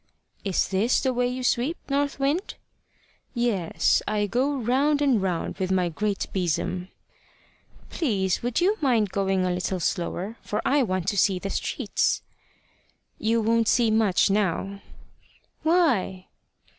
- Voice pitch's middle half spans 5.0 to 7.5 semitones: Yes, average, 5.3 semitones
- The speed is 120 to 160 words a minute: Yes, average, 140 wpm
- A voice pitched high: Yes, high, 215 Hz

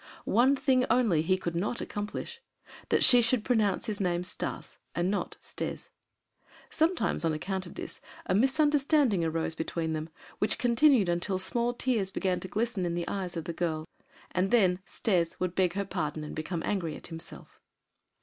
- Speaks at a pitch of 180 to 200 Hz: Yes, high, 190 Hz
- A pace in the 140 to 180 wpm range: Yes, average, 170 wpm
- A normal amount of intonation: No, wide, 5.7 semitones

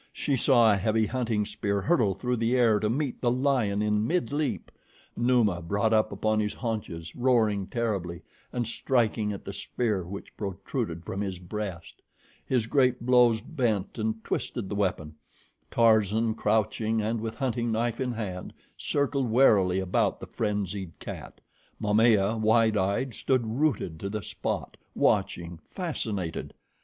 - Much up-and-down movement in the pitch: No, average, 3.2 semitones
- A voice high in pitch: No, low, 110 Hz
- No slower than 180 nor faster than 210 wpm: No, average, 150 wpm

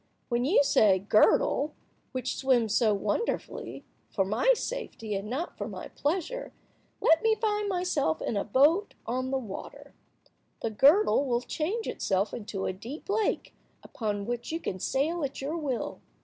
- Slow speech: No, average, 160 wpm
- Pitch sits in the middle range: No, very high, 265 Hz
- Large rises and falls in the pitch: Yes, wide, 7.8 semitones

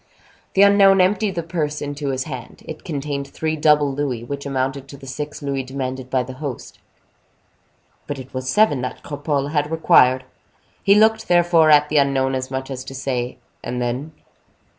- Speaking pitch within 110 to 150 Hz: Yes, medium, 140 Hz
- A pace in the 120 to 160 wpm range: No, average, 180 wpm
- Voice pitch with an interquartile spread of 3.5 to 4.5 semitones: No, average, 3.0 semitones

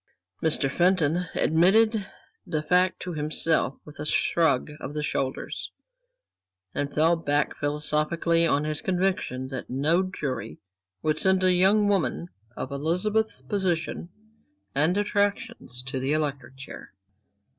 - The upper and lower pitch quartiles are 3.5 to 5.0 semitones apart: Yes, average, 4.1 semitones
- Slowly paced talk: Yes, slow, 125 wpm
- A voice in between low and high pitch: Yes, medium, 160 Hz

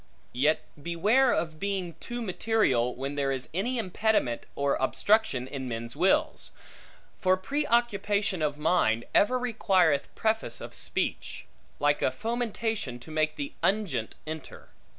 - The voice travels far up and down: Yes, wide, 7.8 semitones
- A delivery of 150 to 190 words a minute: No, slow, 135 wpm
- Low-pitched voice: No, medium, 175 Hz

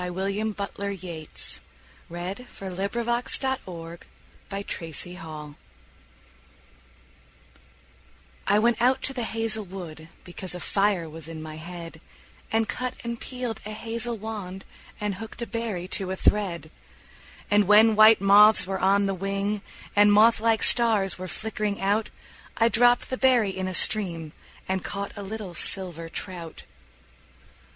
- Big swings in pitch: No, average, 3.6 semitones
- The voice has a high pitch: Yes, high, 200 Hz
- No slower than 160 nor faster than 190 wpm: No, average, 140 wpm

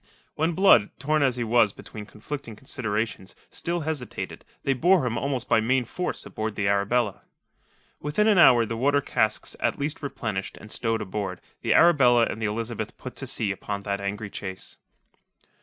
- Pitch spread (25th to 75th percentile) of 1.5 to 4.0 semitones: No, average, 5.1 semitones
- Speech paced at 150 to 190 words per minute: Yes, average, 175 wpm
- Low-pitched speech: Yes, low, 115 Hz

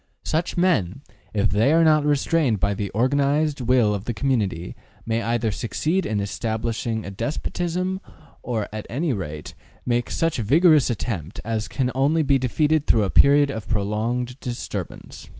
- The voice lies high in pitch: No, low, 120 Hz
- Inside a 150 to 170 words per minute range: Yes, average, 160 wpm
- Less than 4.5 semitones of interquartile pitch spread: No, wide, 5.4 semitones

